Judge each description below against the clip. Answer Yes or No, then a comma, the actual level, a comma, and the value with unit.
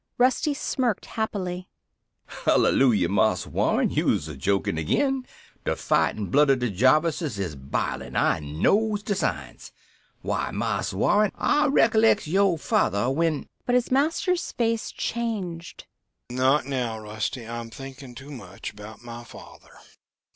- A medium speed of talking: No, slow, 130 wpm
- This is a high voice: No, medium, 140 Hz